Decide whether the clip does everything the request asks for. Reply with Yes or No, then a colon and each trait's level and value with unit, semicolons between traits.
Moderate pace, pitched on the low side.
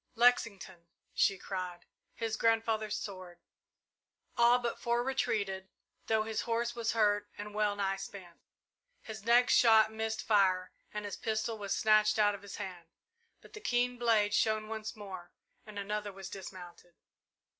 No: average, 150 wpm; high, 210 Hz